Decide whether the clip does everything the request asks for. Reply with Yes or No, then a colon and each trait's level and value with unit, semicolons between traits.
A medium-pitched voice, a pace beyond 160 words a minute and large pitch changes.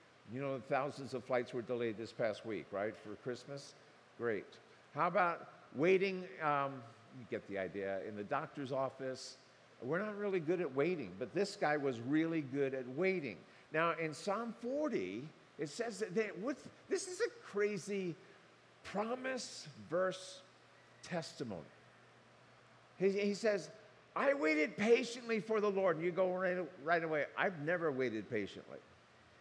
No: medium, 170 Hz; average, 155 wpm; wide, 7.1 semitones